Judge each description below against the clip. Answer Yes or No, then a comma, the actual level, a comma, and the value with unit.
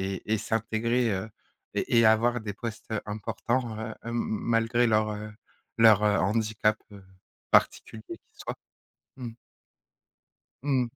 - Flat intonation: Yes, narrow, 1.6 semitones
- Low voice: Yes, low, 110 Hz